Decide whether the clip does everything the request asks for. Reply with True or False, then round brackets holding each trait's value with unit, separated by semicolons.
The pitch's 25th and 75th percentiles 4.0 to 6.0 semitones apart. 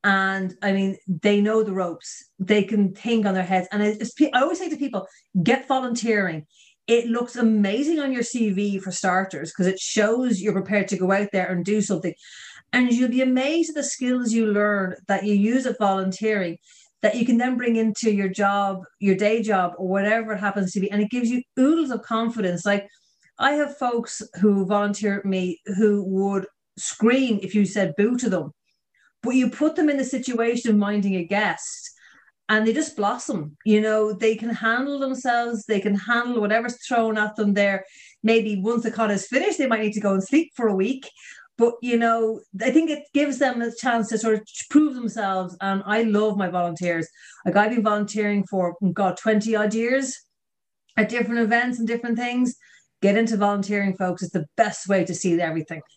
False (3.3 semitones)